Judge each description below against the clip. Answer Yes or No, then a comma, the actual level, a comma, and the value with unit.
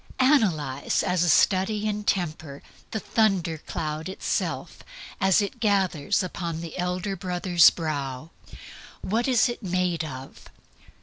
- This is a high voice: No, medium, 180 Hz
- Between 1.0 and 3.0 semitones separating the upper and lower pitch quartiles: No, average, 4.2 semitones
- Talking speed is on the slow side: Yes, slow, 125 wpm